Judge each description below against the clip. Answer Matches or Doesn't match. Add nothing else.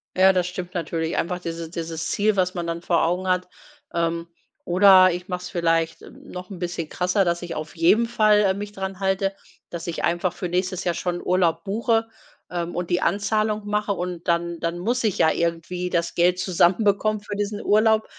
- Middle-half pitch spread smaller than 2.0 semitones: Doesn't match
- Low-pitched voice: Doesn't match